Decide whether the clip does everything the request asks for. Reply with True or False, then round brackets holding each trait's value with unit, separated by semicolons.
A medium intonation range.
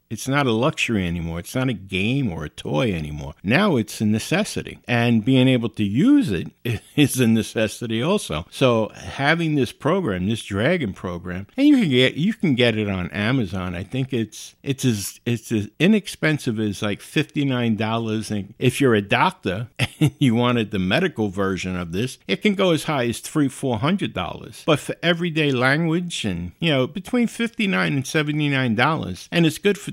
False (6.5 semitones)